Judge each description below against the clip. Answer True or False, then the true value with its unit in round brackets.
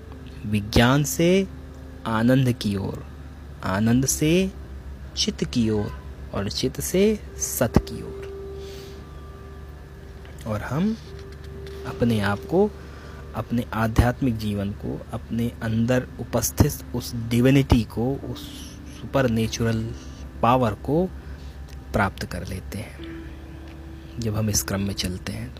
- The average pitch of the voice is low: True (100 Hz)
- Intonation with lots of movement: True (8.1 semitones)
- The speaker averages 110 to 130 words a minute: True (115 wpm)